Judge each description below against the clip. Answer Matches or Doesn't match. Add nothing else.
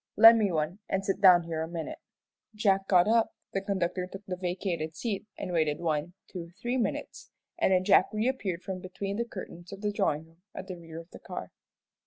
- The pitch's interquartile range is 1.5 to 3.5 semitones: Matches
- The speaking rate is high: Matches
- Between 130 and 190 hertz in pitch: Matches